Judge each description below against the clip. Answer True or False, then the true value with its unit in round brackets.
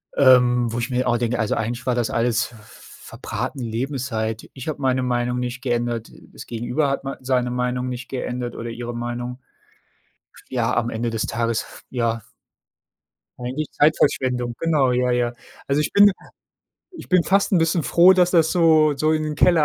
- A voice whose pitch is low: True (125 Hz)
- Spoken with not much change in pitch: False (3.3 semitones)